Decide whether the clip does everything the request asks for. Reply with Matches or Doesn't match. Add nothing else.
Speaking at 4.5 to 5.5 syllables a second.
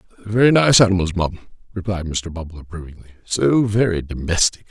Doesn't match